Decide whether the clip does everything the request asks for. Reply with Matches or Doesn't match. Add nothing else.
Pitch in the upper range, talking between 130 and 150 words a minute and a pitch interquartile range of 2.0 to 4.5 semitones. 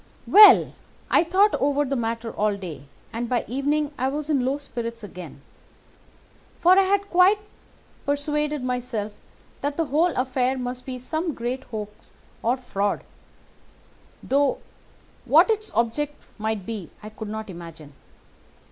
Doesn't match